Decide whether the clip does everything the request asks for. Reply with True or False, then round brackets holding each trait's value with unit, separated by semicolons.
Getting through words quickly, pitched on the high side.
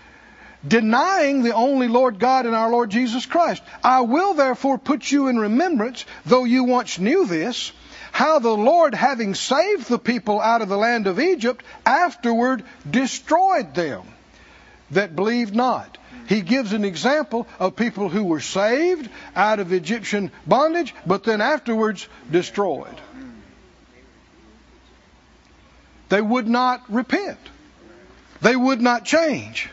False (135 wpm; 245 Hz)